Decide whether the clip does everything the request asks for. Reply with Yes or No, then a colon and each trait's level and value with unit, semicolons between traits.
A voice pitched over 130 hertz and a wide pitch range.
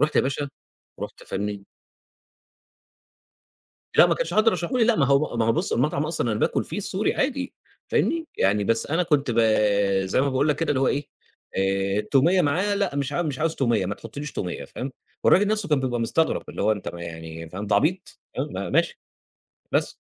Yes: medium, 140 Hz; wide, 8.3 semitones